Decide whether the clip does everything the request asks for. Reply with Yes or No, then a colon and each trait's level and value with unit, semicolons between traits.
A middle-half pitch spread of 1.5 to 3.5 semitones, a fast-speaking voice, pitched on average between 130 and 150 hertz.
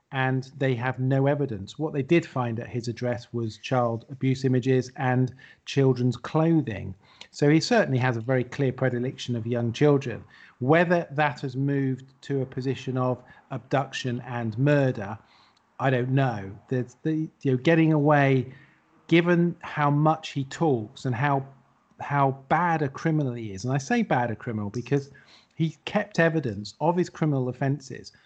No: average, 3.0 semitones; average, 165 wpm; low, 135 Hz